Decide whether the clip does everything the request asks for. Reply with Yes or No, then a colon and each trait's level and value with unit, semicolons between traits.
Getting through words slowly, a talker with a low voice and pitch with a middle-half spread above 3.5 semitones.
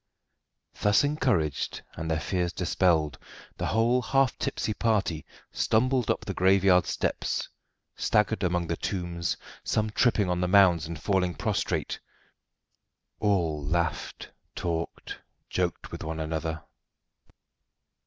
Yes: slow, 115 wpm; very low, 90 Hz; average, 4.2 semitones